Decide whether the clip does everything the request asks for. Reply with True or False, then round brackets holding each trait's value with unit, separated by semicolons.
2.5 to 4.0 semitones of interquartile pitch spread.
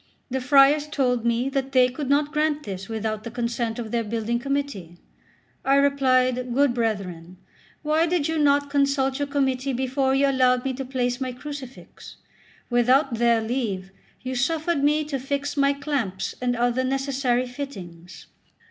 True (2.9 semitones)